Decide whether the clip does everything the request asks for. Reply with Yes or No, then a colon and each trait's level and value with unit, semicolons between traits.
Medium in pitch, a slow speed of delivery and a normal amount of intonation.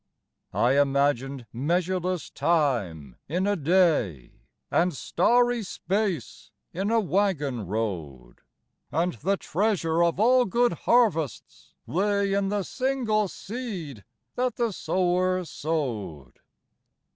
No: medium, 175 Hz; slow, 105 wpm; wide, 6.8 semitones